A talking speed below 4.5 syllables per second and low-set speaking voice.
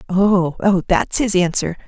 No: 4.0 syllables/s; medium, 185 Hz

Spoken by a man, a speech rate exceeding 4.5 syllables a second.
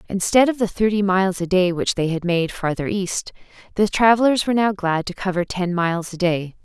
No: female; 5.6 syllables/s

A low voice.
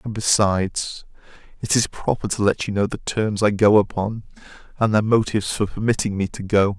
Yes: low, 105 Hz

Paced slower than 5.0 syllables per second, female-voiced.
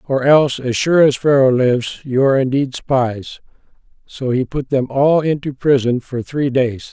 No: 4.6 syllables/s; male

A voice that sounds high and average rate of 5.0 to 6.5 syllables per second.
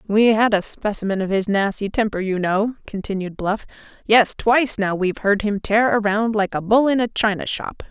Yes: high, 210 Hz; 5.2 syllables/s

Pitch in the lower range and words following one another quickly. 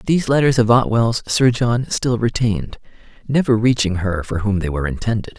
No: low, 110 Hz; average, 180 wpm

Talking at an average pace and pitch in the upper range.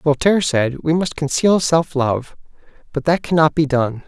No: average, 190 wpm; medium, 150 Hz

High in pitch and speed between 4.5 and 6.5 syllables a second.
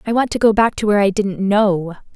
Yes: high, 205 Hz; 6.0 syllables/s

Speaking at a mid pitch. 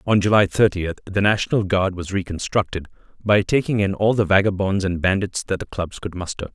No: very low, 95 Hz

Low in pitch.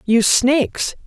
No: very high, 255 Hz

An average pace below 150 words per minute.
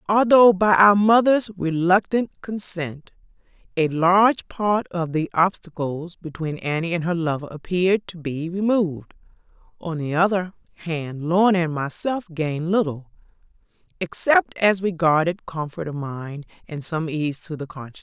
Yes: average, 140 wpm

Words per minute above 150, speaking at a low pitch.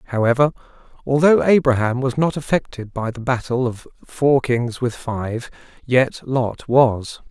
No: average, 140 wpm; low, 125 Hz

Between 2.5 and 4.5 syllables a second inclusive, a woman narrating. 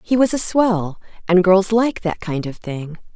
Yes: 4.2 syllables/s; female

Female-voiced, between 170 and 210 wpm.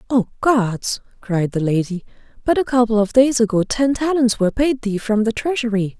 Yes: female; average, 190 wpm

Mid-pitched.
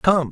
Yes: medium, 160 Hz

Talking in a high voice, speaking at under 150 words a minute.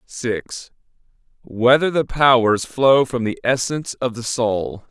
No: low, 125 Hz; slow, 135 wpm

